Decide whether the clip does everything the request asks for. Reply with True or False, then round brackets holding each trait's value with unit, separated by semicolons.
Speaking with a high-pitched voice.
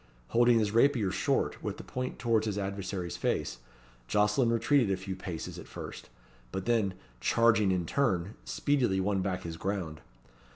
False (100 Hz)